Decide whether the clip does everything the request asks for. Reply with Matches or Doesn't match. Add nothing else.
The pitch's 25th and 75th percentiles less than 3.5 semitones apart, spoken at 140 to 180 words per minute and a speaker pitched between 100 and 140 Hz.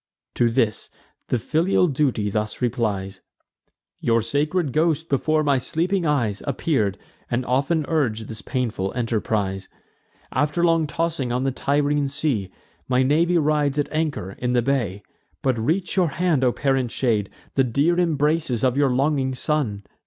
Doesn't match